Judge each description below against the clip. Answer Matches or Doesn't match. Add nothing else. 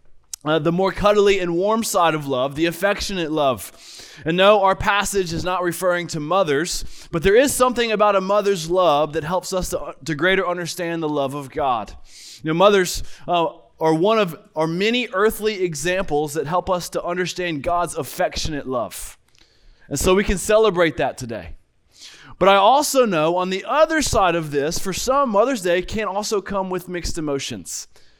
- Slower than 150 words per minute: Doesn't match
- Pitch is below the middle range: Doesn't match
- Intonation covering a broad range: Doesn't match